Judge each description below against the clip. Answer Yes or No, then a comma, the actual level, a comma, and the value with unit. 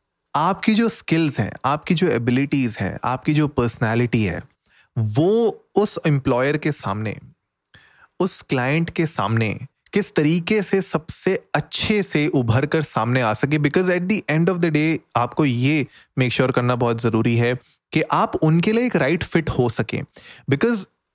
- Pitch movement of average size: No, wide, 5.8 semitones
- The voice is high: No, medium, 145 Hz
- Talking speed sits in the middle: Yes, average, 165 wpm